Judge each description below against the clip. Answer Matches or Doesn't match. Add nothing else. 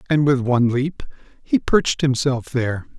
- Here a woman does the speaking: Doesn't match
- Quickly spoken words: Doesn't match